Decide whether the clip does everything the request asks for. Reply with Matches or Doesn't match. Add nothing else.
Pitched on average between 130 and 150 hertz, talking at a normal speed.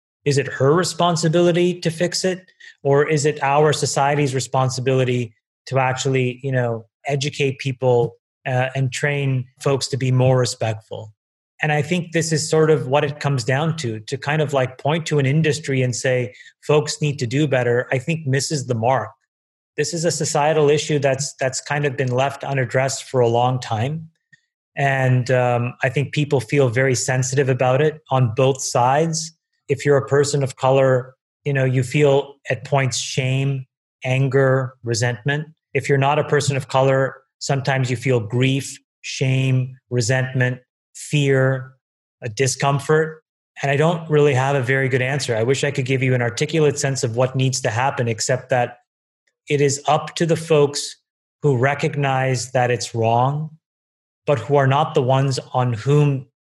Matches